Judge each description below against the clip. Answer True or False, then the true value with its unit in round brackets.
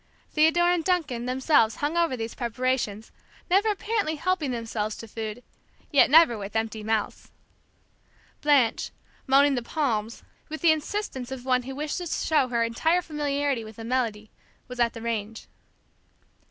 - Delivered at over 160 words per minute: False (155 wpm)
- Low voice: False (255 Hz)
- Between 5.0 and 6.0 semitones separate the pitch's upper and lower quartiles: True (5.3 semitones)